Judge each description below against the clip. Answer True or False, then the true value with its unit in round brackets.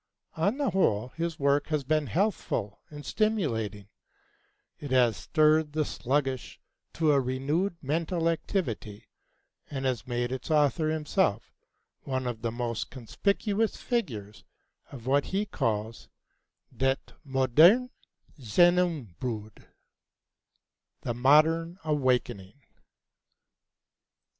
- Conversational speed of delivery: False (105 wpm)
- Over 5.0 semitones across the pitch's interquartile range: True (5.4 semitones)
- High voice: False (140 Hz)